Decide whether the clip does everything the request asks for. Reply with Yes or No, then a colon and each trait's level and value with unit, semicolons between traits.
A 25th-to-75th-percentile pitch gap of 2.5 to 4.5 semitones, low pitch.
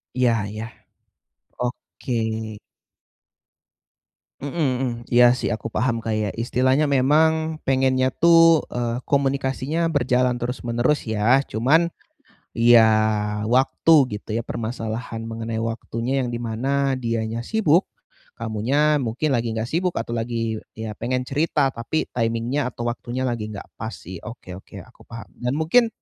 Yes: average, 3.3 semitones; low, 125 Hz